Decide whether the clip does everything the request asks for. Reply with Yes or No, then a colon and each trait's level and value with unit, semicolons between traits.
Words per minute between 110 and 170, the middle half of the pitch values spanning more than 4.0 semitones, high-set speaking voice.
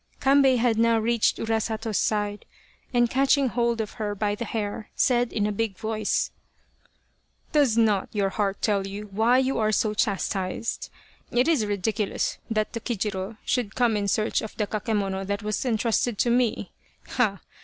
No: average, 165 wpm; narrow, 2.4 semitones; high, 220 Hz